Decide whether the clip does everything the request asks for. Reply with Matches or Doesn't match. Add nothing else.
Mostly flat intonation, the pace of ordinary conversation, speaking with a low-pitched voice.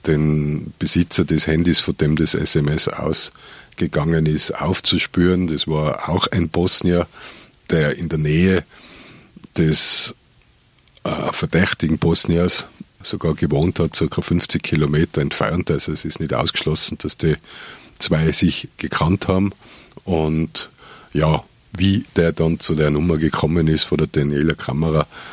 Matches